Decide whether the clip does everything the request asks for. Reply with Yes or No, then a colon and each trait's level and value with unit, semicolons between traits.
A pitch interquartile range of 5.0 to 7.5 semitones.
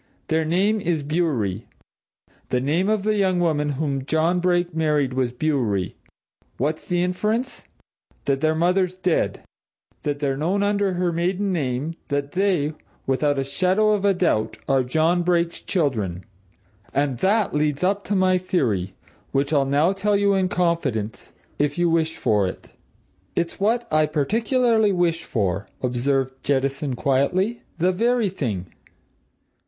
Yes: average, 5.3 semitones